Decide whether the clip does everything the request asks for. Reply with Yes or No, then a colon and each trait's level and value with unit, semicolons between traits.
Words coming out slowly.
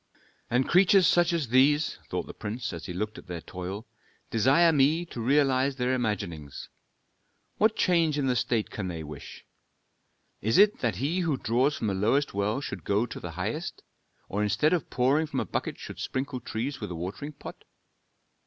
No: average, 185 wpm